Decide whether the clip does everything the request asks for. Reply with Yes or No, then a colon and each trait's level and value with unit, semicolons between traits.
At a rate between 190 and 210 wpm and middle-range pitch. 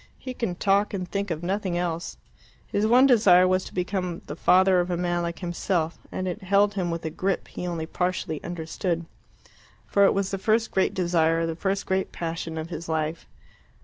Yes: average, 200 wpm; medium, 180 Hz